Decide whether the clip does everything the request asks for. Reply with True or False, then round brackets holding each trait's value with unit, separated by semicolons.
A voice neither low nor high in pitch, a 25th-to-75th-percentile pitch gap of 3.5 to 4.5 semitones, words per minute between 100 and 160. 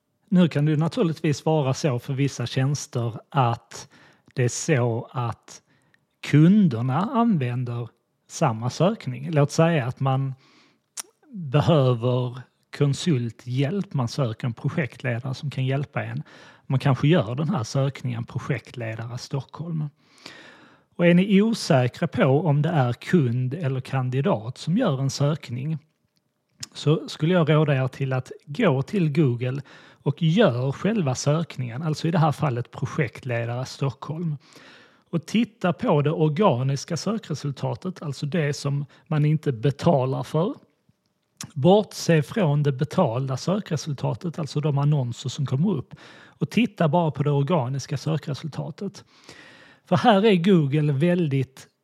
True (145 Hz; 3.9 semitones; 130 wpm)